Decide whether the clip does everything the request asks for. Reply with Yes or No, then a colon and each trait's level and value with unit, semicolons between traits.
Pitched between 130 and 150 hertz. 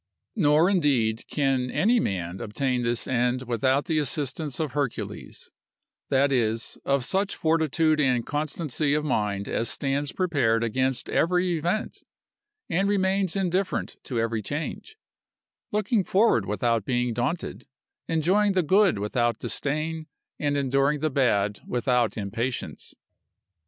Yes: medium, 140 Hz